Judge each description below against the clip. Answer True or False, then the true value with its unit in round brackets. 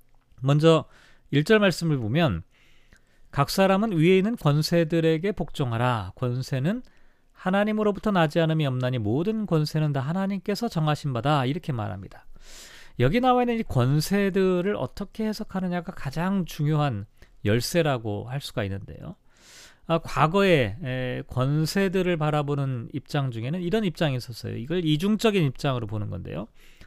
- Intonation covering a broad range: True (6.7 semitones)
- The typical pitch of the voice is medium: True (155 Hz)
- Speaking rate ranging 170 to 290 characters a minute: False (315 characters per minute)